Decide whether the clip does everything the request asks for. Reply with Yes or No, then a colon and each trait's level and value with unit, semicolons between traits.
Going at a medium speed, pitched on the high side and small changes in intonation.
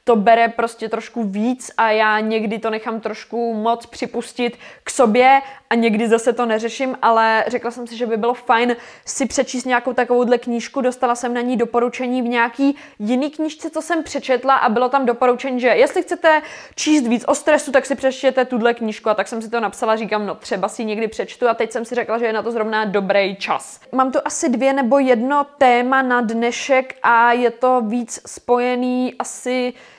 No: fast, 200 wpm; high, 245 Hz; narrow, 2.2 semitones